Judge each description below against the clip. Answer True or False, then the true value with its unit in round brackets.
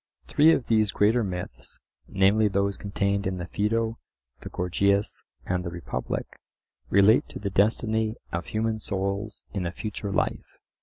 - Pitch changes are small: True (2.1 semitones)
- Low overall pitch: True (100 Hz)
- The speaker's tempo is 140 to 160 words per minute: True (150 wpm)